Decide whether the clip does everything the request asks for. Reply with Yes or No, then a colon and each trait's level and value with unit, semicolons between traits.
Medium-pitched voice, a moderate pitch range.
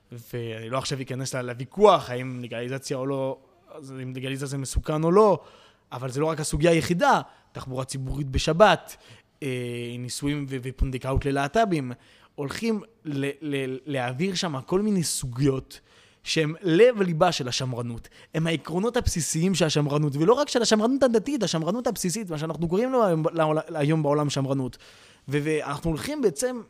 Yes: medium, 145 Hz; average, 4.5 semitones